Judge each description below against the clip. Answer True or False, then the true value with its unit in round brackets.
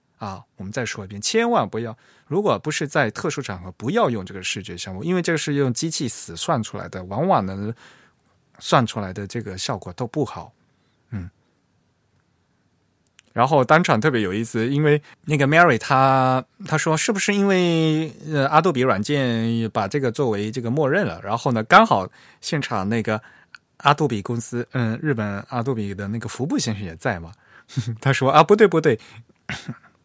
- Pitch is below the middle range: True (120 Hz)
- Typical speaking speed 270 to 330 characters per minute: True (275 characters per minute)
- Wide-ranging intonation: True (5.8 semitones)